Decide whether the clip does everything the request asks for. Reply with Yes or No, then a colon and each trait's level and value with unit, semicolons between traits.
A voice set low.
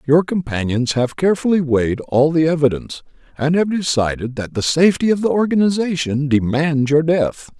No: medium, 155 Hz